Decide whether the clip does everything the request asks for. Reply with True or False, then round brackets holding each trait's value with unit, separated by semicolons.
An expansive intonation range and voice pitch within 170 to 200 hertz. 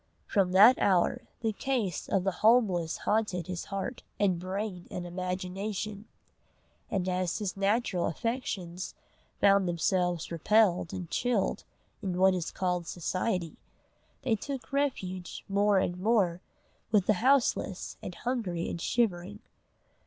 False (3.2 semitones; 190 Hz)